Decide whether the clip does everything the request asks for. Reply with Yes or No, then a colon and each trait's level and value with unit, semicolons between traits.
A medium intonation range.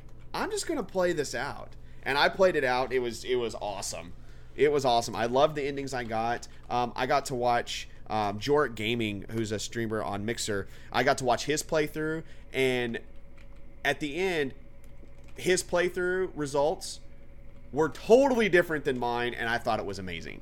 No: wide, 6.3 semitones